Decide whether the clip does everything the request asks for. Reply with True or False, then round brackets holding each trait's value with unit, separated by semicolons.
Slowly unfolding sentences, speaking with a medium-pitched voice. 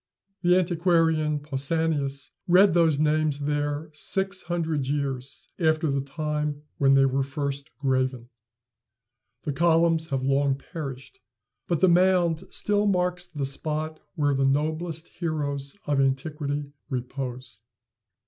True (120 wpm; 150 Hz)